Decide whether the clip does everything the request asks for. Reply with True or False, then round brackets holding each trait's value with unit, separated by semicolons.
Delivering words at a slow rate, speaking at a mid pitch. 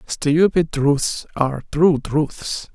True (110 wpm; 150 Hz)